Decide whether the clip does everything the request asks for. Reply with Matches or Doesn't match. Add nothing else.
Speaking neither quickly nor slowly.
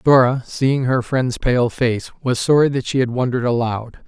Matches